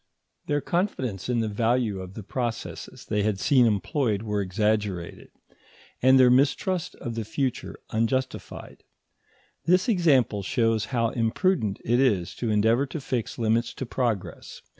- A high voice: No, low, 115 Hz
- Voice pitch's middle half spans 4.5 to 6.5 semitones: No, average, 3.8 semitones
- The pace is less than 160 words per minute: Yes, average, 140 wpm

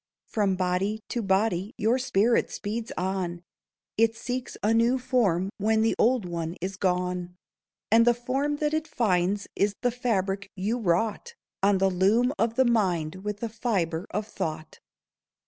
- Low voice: No, high, 205 Hz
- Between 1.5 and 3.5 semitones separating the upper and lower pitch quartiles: No, average, 4.1 semitones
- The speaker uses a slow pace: No, average, 160 wpm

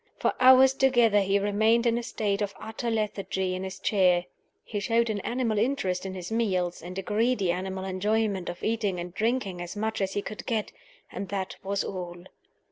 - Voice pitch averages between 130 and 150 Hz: No, high, 205 Hz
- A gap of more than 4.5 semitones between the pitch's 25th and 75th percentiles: No, average, 3.2 semitones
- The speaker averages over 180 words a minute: Yes, average, 195 wpm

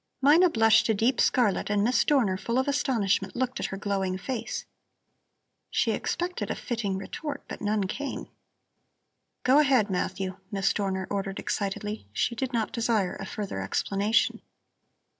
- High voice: Yes, high, 215 Hz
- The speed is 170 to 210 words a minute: No, average, 150 wpm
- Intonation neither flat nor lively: Yes, average, 4.6 semitones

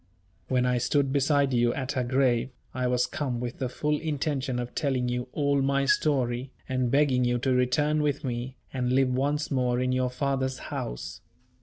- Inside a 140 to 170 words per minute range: No, average, 185 wpm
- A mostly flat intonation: Yes, narrow, 2.0 semitones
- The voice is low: Yes, low, 130 Hz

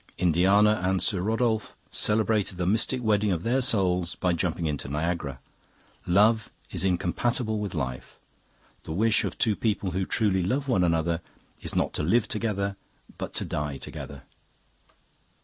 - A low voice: Yes, very low, 95 Hz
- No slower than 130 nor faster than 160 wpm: Yes, average, 150 wpm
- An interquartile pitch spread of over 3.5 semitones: Yes, average, 3.9 semitones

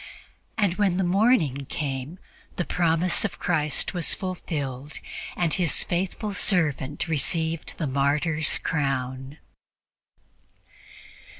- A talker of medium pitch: Yes, medium, 160 Hz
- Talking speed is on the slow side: Yes, slow, 100 wpm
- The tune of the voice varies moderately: Yes, average, 4.1 semitones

